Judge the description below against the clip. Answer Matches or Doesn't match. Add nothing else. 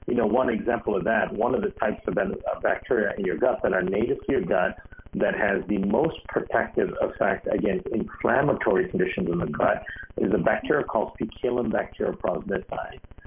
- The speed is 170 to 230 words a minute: Matches